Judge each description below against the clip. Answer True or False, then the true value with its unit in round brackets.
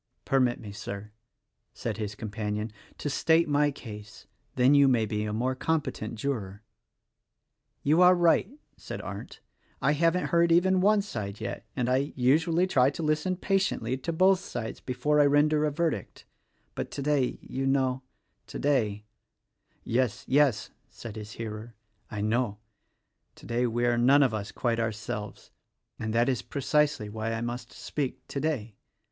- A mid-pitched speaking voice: False (125 Hz)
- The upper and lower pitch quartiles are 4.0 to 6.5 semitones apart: True (5.2 semitones)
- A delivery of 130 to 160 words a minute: True (155 wpm)